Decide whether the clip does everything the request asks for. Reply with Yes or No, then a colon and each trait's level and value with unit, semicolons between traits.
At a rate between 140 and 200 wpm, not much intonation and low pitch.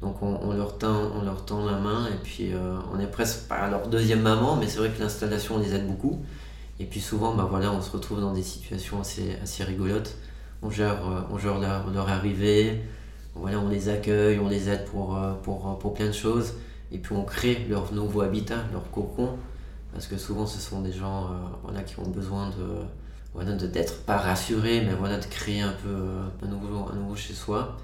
No: average, 215 wpm; narrow, 1.7 semitones; low, 100 Hz